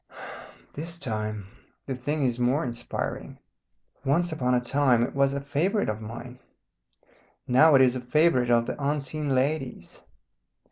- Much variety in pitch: No, average, 3.3 semitones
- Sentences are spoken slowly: No, average, 145 wpm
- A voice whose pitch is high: No, low, 130 Hz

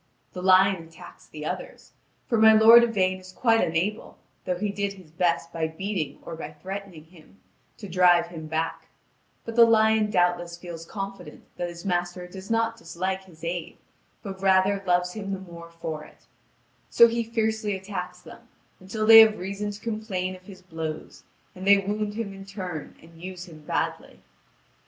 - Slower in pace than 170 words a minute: No, average, 175 wpm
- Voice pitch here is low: No, high, 190 Hz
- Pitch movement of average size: Yes, average, 3.3 semitones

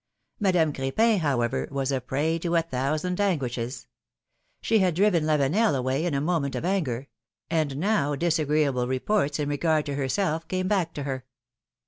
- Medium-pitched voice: Yes, medium, 155 Hz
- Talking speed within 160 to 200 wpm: Yes, average, 170 wpm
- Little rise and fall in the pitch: No, average, 4.5 semitones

